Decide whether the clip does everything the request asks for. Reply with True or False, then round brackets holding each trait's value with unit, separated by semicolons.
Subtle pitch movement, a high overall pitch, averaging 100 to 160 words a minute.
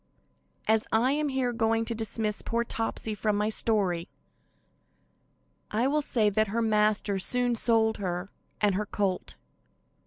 True (1.9 semitones; 220 Hz; 145 wpm)